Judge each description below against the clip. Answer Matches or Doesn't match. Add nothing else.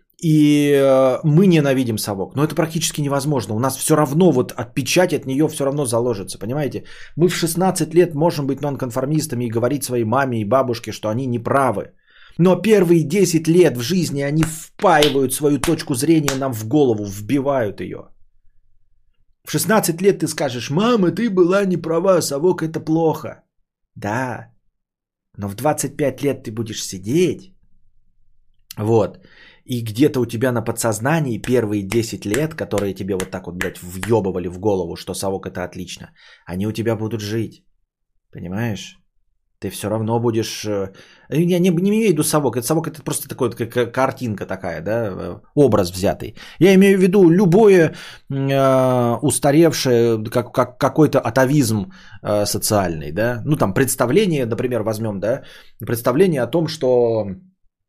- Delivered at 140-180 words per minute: Matches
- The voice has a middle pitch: Doesn't match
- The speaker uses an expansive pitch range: Matches